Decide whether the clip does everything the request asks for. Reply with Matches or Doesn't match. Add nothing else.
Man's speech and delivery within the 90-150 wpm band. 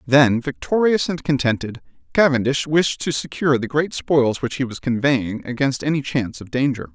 Doesn't match